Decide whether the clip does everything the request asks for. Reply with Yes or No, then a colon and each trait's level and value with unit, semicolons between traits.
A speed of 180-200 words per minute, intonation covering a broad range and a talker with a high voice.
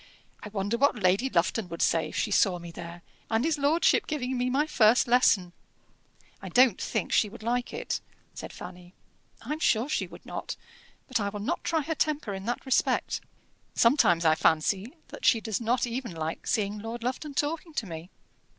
Yes: average, 190 wpm; wide, 5.7 semitones; high, 225 Hz